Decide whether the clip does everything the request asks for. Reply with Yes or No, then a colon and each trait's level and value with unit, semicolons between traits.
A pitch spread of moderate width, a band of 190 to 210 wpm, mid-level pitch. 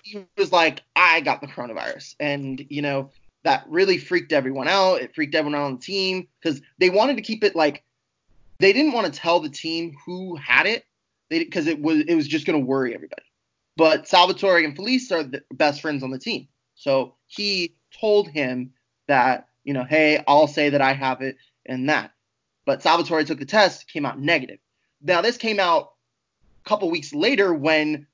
No: wide, 5.7 semitones; average, 200 wpm; medium, 160 Hz